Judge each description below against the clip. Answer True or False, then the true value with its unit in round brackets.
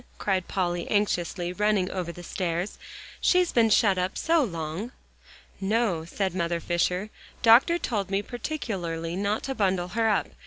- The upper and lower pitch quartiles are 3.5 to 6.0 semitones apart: True (4.0 semitones)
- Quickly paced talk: False (150 wpm)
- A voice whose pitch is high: True (195 Hz)